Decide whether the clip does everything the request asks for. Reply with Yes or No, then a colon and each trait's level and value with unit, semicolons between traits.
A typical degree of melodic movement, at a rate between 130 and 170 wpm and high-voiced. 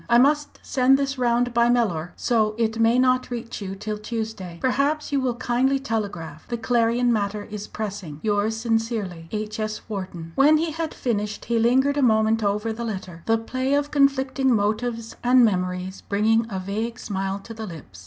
No: average, 3.4 semitones; average, 180 wpm; high, 225 Hz